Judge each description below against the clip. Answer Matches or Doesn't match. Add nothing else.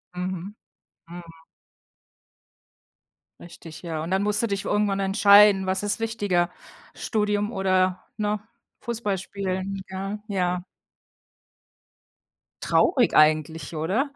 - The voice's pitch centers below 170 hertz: Doesn't match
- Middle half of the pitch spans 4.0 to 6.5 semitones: Doesn't match